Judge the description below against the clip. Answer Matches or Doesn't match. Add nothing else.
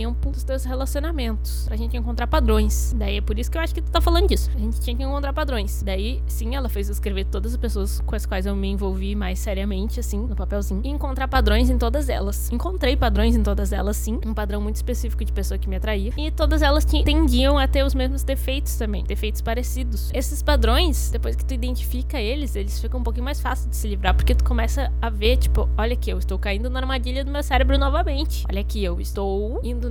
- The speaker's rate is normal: Doesn't match